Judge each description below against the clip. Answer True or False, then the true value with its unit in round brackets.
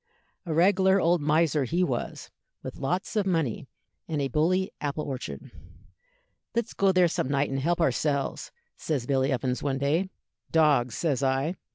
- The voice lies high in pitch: False (150 Hz)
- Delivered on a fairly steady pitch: False (4.5 semitones)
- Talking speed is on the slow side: False (160 wpm)